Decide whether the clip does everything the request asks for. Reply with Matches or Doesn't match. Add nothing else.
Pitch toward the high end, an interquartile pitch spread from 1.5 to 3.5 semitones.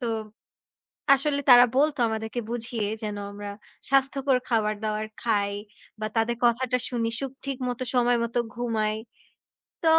Matches